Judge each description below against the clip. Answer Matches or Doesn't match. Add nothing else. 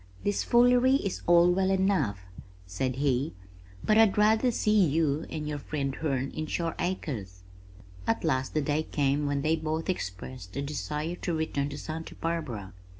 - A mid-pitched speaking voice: Matches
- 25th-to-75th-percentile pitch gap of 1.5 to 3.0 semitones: Doesn't match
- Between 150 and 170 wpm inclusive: Matches